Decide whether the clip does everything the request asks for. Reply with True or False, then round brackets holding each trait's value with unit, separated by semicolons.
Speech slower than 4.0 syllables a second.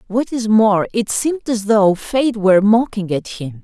False (4.4 syllables/s)